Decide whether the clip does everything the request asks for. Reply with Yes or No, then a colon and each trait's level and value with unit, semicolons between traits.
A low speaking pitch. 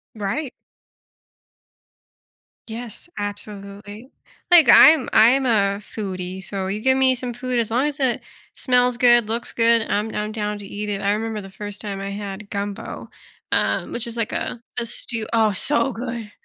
No: high, 220 Hz